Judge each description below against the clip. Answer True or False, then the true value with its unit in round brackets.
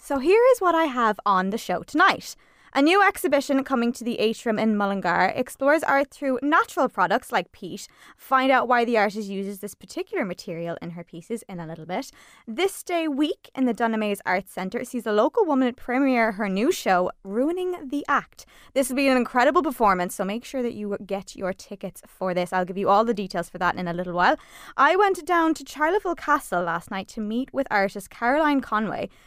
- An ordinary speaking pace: False (210 wpm)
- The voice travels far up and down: True (6.4 semitones)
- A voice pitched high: True (235 Hz)